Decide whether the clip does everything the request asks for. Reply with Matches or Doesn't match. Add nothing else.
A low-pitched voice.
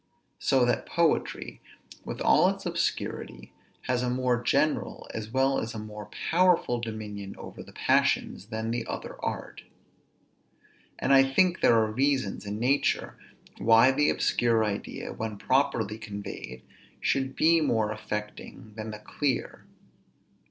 Matches